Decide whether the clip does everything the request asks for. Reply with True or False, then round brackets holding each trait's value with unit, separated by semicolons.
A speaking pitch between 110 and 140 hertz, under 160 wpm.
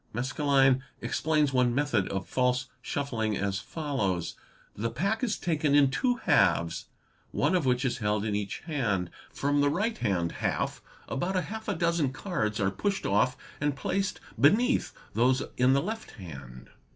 False (135 Hz; 165 wpm)